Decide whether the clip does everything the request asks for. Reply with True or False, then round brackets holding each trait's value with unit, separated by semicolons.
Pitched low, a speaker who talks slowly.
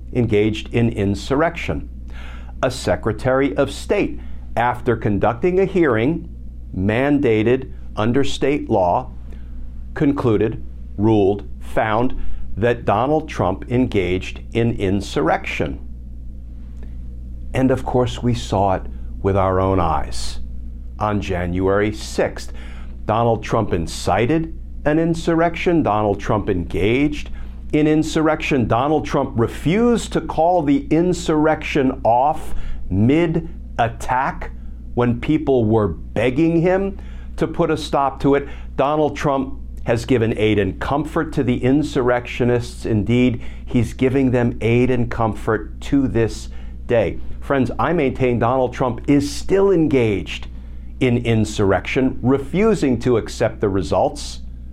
True (115 Hz; 115 wpm)